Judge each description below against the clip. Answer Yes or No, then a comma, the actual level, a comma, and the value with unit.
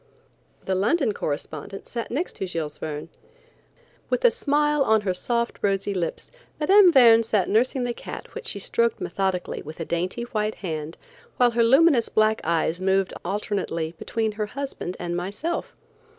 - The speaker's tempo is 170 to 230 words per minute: No, average, 160 wpm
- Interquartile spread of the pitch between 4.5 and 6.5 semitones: Yes, average, 5.1 semitones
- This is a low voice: No, high, 210 Hz